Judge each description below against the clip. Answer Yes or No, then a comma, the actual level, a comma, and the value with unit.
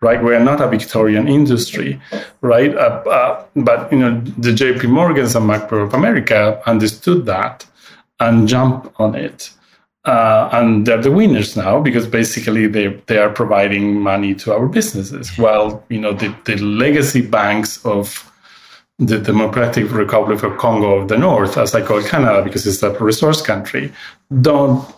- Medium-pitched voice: No, low, 110 Hz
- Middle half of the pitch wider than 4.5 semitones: No, average, 2.9 semitones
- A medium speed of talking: Yes, average, 160 wpm